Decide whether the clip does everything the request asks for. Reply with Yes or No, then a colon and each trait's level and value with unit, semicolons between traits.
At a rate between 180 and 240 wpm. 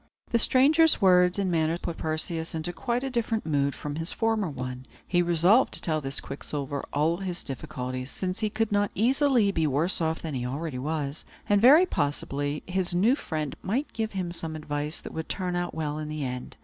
Yes: average, 200 wpm